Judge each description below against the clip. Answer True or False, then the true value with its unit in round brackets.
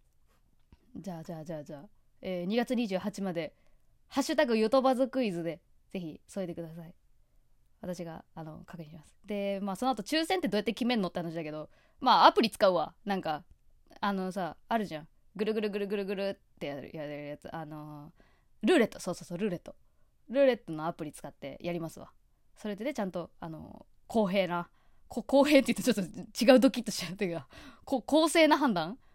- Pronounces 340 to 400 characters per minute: True (390 characters per minute)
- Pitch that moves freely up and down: True (5.9 semitones)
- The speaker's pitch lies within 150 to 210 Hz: True (190 Hz)